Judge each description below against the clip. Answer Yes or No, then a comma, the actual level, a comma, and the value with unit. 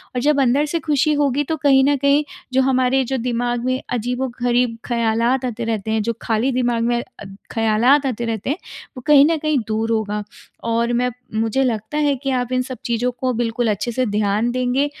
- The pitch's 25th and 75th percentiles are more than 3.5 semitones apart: No, average, 2.8 semitones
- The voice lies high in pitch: Yes, high, 245 Hz